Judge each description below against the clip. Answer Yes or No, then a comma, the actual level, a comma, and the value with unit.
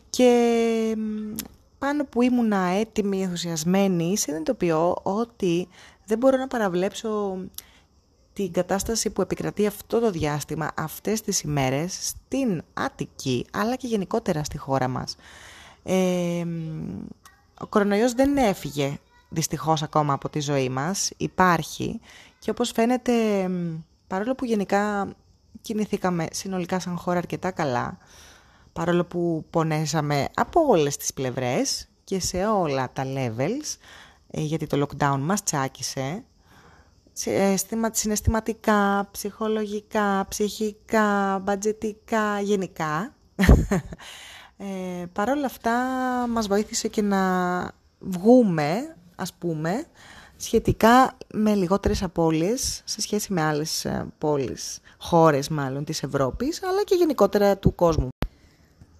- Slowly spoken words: Yes, slow, 105 wpm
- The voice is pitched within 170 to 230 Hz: Yes, high, 190 Hz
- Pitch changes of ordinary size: No, wide, 5.7 semitones